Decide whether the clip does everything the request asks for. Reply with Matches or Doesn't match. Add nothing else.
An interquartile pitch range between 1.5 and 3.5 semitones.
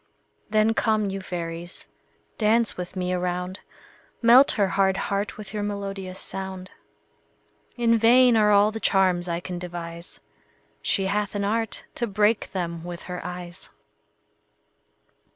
Matches